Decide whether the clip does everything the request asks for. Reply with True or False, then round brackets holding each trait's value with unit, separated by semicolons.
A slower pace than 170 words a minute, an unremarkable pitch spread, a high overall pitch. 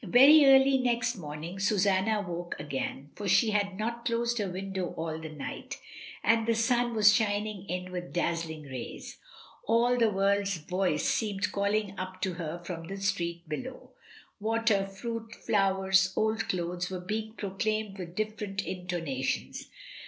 True (150 wpm; 3.7 semitones; 195 Hz)